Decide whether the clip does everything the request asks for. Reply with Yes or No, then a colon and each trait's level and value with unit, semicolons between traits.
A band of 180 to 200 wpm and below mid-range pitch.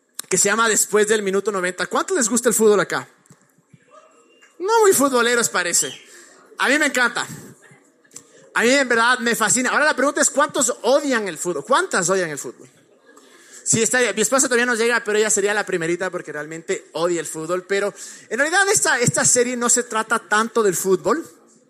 No: fast, 190 wpm; high, 225 Hz